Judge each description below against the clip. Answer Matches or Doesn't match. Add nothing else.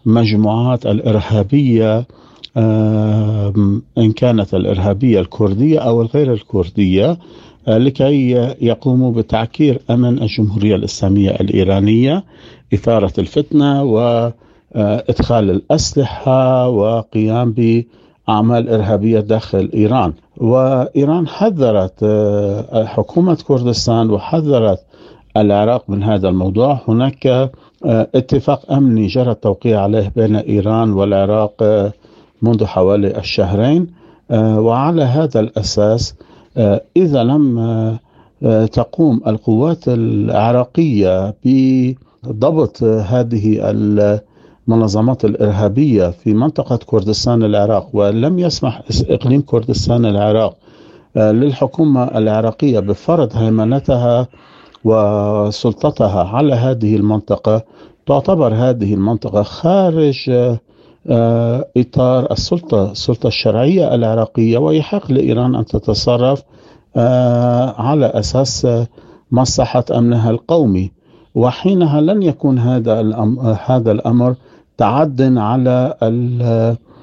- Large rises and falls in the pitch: Doesn't match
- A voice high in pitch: Doesn't match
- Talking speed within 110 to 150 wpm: Doesn't match